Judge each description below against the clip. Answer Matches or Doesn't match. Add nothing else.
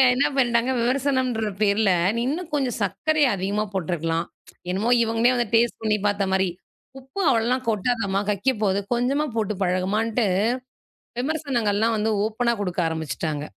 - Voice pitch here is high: Matches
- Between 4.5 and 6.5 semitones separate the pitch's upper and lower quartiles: Doesn't match